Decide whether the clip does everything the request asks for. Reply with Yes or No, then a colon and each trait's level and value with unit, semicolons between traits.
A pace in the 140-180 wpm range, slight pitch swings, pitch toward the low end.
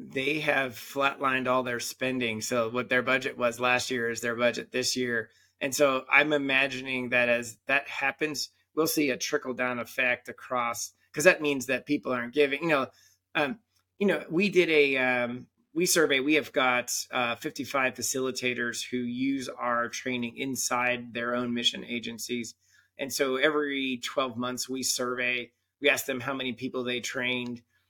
Yes: average, 175 wpm; narrow, 2.2 semitones; low, 125 Hz